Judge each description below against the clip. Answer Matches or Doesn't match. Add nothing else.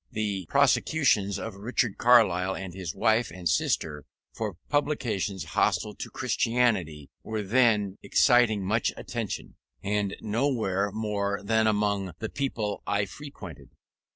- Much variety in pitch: Doesn't match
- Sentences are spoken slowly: Matches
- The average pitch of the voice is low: Matches